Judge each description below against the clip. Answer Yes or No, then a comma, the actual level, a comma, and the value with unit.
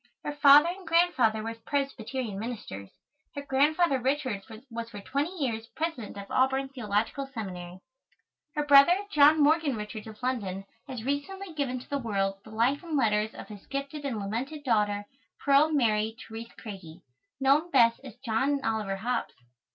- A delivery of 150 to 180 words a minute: Yes, average, 160 wpm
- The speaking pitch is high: Yes, very high, 250 Hz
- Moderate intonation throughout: Yes, average, 4.7 semitones